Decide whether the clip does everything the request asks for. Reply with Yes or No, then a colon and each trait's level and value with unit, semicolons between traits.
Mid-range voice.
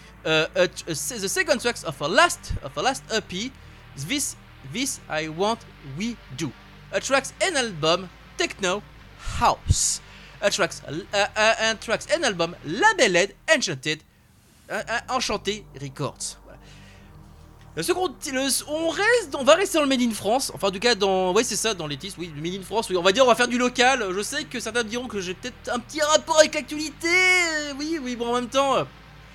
No: high, 220 Hz